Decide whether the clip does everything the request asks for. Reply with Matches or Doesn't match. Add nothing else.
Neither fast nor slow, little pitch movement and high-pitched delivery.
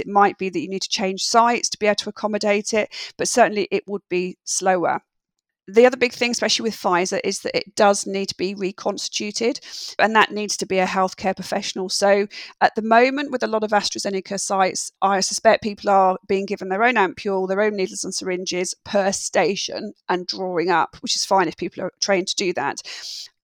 Doesn't match